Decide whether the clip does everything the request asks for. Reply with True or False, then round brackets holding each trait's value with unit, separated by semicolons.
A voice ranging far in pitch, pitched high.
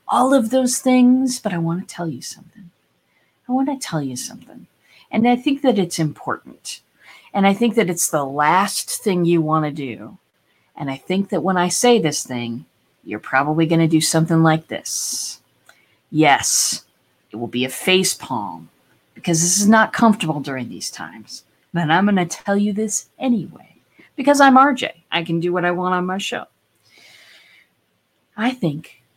False (5.9 semitones; 180 Hz)